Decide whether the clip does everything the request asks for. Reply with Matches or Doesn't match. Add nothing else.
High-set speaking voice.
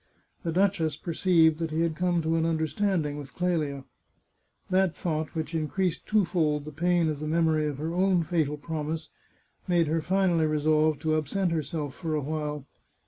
Doesn't match